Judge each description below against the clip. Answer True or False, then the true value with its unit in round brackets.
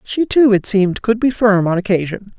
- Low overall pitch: False (210 Hz)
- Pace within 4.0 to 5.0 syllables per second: False (5.3 syllables/s)